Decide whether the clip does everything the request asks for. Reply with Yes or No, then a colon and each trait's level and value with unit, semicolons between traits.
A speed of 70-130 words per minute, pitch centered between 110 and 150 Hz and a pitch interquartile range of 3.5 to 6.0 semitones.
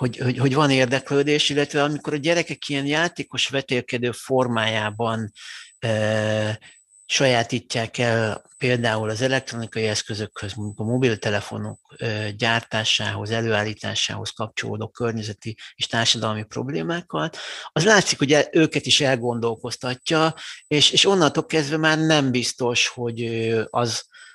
Yes: average, 110 wpm; low, 120 Hz; average, 4.4 semitones